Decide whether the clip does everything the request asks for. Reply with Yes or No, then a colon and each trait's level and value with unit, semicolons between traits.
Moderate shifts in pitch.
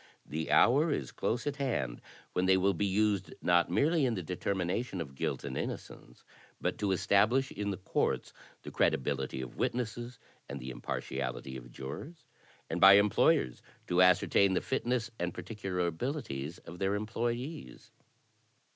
No: wide, 6.6 semitones